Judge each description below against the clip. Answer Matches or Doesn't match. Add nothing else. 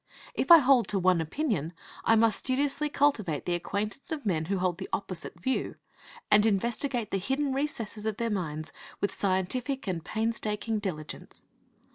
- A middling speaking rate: Matches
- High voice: Matches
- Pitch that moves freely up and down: Matches